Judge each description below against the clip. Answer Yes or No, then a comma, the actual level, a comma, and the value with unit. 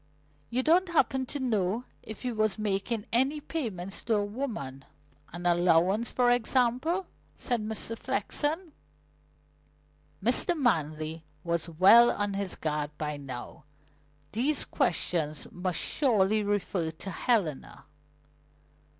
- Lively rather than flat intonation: Yes, wide, 6.1 semitones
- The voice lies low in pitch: No, high, 205 Hz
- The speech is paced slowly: Yes, slow, 115 wpm